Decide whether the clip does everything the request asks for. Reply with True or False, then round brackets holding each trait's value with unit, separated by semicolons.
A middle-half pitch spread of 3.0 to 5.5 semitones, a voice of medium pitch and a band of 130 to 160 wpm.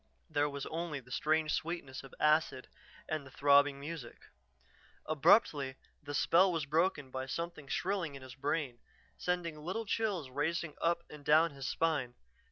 True (3.3 semitones; 150 Hz; 155 wpm)